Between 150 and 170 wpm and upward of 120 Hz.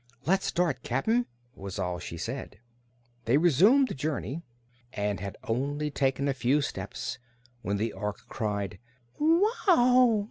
No: slow, 135 wpm; medium, 140 Hz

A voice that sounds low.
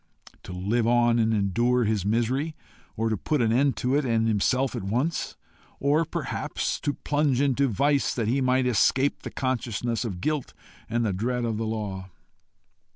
Yes: low, 120 Hz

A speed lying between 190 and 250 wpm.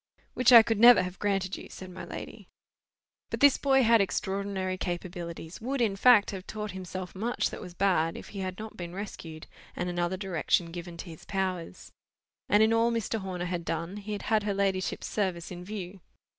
Yes: average, 200 wpm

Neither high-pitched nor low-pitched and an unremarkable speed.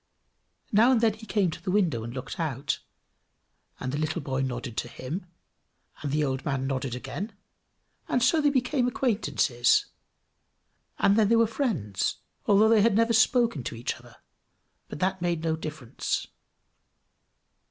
Yes: medium, 170 Hz; average, 160 wpm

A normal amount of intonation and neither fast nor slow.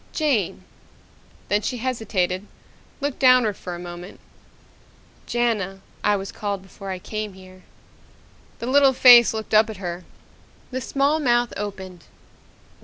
No: average, 4.5 semitones; slow, 130 wpm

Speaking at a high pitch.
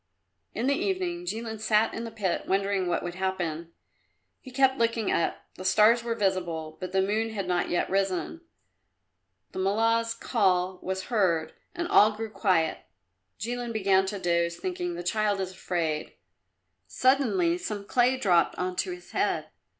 Yes: high, 200 Hz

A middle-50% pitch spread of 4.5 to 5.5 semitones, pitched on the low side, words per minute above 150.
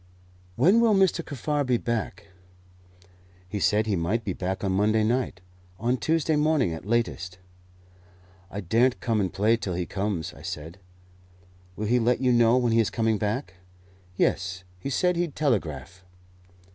Yes: average, 5.2 semitones; low, 110 Hz; average, 160 wpm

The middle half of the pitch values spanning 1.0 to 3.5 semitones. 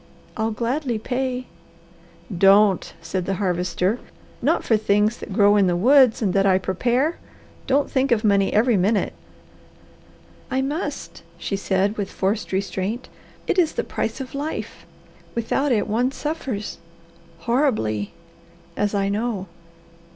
No: average, 4.6 semitones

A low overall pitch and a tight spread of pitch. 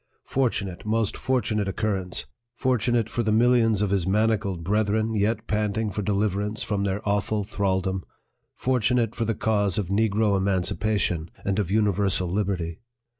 Yes: low, 105 Hz; narrow, 2.2 semitones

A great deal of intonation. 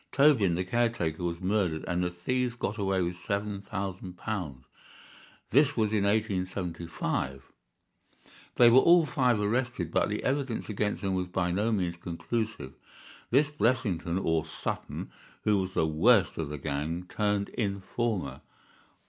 No: average, 4.6 semitones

